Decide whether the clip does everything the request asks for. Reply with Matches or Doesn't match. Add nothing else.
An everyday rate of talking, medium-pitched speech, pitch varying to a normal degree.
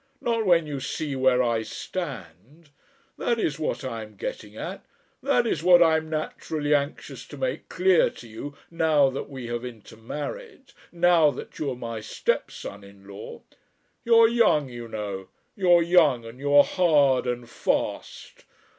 Doesn't match